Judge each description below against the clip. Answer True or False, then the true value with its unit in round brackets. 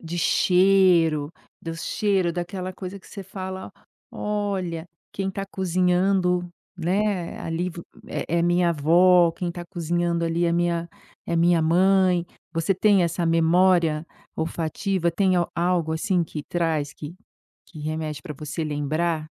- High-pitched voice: False (175 Hz)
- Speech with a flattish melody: True (2.2 semitones)